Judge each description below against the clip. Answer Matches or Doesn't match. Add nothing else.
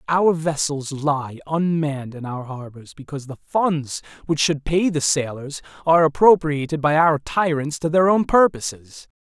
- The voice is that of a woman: Doesn't match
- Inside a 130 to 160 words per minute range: Matches